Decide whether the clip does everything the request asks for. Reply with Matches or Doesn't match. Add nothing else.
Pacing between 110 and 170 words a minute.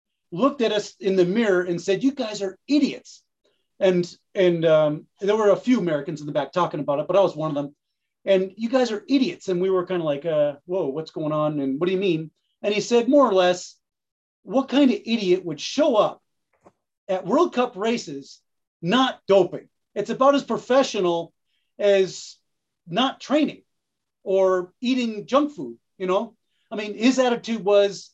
Doesn't match